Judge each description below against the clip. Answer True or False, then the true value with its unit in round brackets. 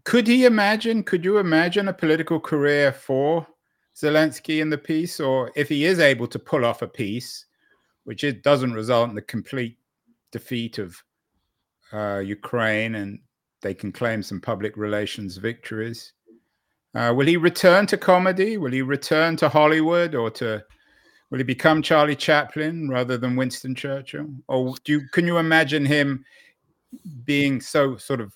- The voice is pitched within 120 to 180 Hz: True (140 Hz)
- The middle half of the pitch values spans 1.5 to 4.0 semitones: False (5.2 semitones)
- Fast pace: False (160 wpm)